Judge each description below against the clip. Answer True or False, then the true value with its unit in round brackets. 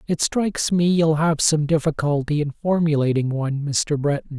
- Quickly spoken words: False (165 wpm)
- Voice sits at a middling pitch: True (155 Hz)